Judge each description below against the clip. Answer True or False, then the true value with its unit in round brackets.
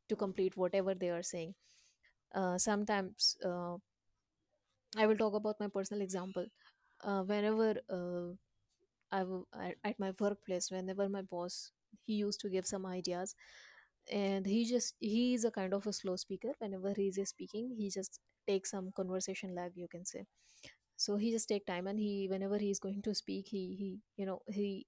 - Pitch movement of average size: False (1.9 semitones)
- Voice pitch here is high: True (195 Hz)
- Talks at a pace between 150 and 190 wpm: True (185 wpm)